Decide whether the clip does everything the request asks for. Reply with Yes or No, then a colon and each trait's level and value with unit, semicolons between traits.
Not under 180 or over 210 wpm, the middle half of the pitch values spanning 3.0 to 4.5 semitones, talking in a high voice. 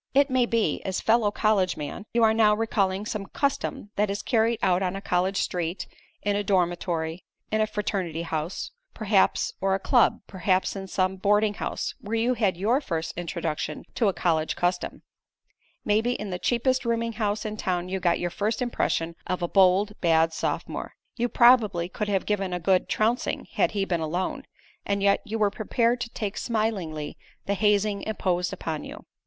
Yes: average, 185 wpm; average, 3.5 semitones; high, 200 Hz